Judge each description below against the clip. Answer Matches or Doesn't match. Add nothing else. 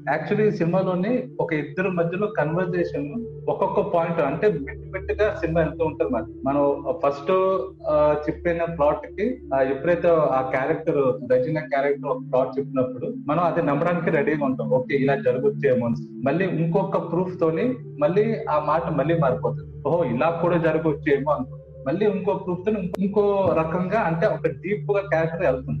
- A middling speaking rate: Doesn't match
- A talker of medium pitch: Matches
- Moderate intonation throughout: Matches